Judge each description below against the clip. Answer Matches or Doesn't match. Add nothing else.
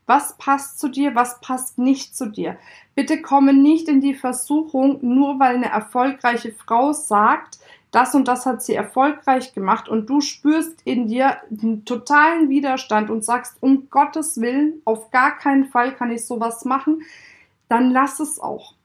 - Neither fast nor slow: Matches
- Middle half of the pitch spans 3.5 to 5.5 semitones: Doesn't match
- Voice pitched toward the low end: Doesn't match